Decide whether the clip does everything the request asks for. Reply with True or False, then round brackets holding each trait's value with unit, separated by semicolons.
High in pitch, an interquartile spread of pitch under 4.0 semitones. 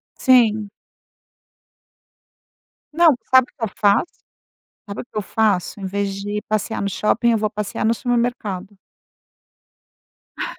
True (215 Hz; 2.9 semitones)